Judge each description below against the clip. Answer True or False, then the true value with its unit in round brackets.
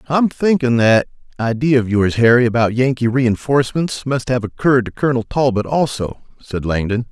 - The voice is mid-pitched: False (125 Hz)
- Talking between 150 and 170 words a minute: True (160 wpm)